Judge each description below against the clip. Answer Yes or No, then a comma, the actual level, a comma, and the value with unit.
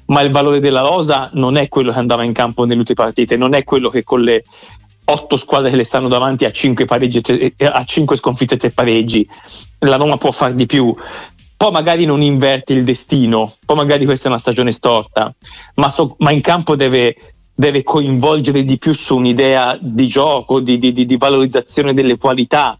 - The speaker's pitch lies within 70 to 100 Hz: No, low, 130 Hz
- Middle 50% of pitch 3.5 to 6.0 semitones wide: No, narrow, 2.5 semitones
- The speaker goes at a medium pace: No, fast, 190 wpm